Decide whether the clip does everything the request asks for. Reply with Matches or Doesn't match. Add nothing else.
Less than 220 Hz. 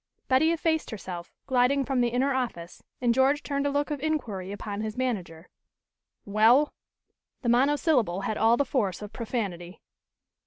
Doesn't match